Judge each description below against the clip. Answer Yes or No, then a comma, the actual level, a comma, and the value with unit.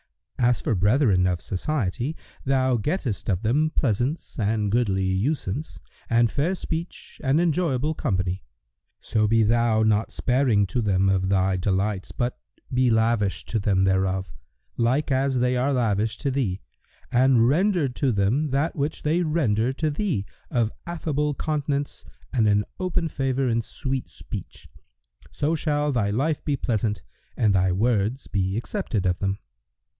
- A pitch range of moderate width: No, wide, 5.8 semitones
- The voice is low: Yes, low, 120 Hz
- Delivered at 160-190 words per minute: No, average, 150 wpm